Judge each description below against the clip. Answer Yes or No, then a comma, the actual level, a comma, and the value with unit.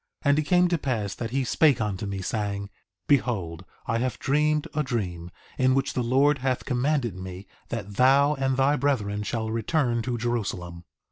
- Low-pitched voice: Yes, low, 120 Hz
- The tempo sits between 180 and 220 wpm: Yes, average, 190 wpm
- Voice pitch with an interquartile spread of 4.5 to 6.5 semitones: Yes, average, 5.1 semitones